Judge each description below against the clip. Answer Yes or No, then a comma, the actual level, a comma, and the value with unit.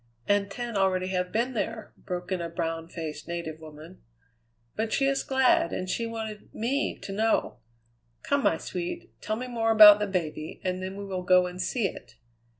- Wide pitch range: No, average, 4.1 semitones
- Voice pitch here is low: No, high, 195 Hz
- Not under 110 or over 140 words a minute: No, average, 190 wpm